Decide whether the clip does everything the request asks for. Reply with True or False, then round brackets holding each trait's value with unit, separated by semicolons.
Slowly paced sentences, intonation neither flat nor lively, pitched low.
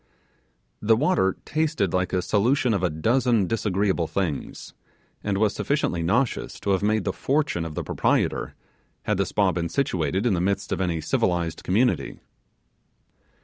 False (155 wpm; 4.3 semitones; 100 Hz)